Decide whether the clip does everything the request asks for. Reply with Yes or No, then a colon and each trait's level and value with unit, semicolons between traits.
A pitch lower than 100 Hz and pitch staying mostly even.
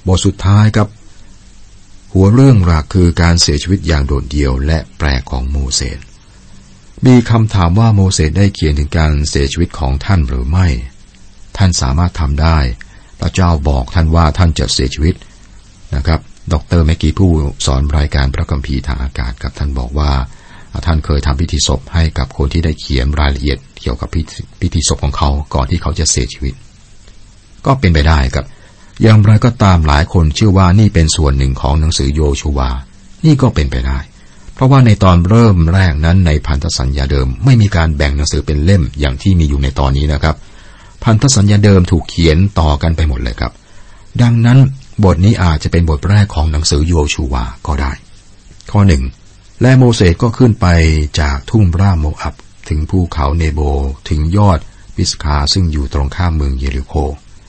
No: very low, 80 Hz; average, 5.2 semitones